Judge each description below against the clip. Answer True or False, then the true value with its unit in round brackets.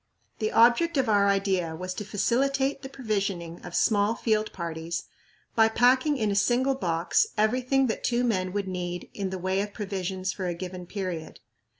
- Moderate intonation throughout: True (4.6 semitones)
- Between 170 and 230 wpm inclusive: True (180 wpm)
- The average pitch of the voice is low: False (205 Hz)